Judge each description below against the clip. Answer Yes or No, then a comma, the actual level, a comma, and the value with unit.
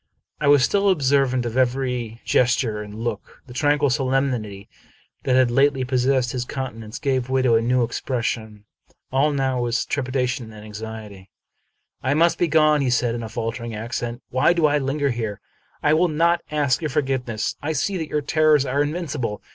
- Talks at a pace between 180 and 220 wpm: Yes, average, 185 wpm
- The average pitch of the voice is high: No, low, 130 Hz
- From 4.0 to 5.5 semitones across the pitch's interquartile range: No, average, 3.6 semitones